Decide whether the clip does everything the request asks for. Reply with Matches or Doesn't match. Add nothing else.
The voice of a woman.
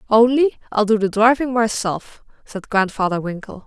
Matches